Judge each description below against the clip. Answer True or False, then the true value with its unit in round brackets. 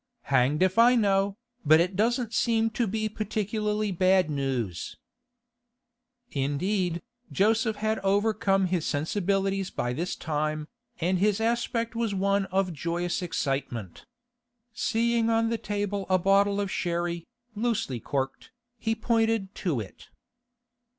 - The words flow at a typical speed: False (125 wpm)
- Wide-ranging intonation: False (4.4 semitones)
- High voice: True (195 Hz)